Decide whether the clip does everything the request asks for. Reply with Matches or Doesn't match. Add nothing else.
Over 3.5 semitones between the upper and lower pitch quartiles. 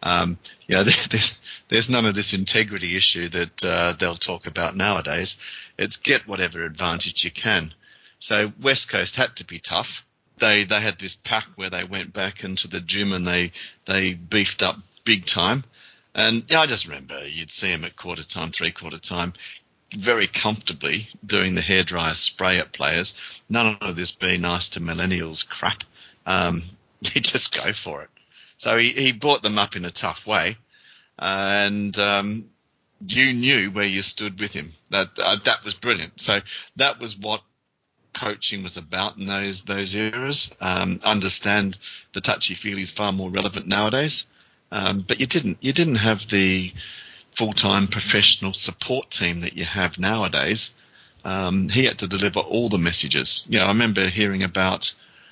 Doesn't match